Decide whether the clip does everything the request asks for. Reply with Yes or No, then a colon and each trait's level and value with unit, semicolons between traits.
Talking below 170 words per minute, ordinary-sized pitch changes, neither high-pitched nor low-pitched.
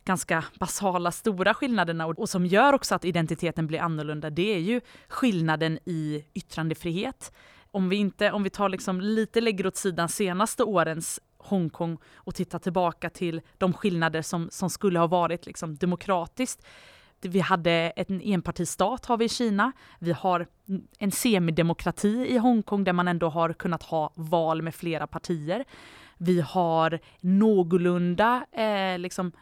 Yes: average, 150 wpm; average, 3.3 semitones; medium, 180 Hz